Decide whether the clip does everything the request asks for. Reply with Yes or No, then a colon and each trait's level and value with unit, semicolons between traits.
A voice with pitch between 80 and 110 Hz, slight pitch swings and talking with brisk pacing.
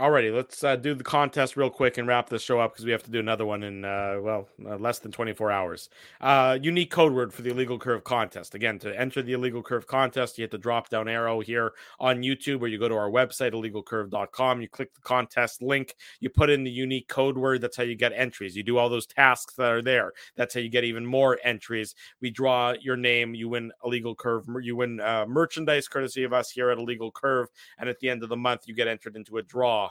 No: low, 120 Hz; narrow, 2.0 semitones; fast, 250 wpm